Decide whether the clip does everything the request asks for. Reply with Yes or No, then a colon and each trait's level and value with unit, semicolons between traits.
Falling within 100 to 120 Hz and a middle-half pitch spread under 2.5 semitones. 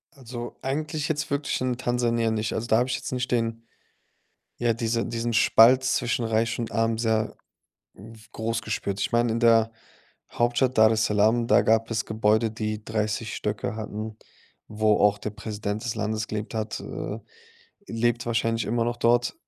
Yes: low, 115 Hz; narrow, 1.5 semitones